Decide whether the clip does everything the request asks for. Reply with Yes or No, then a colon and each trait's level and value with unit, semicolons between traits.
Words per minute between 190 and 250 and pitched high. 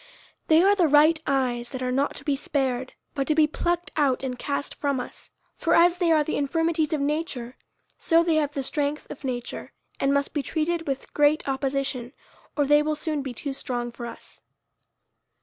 Yes: average, 200 wpm; very high, 285 Hz